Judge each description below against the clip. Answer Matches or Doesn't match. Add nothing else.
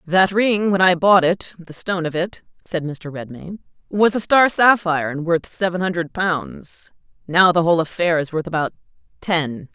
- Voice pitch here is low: Doesn't match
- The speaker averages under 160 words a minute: Doesn't match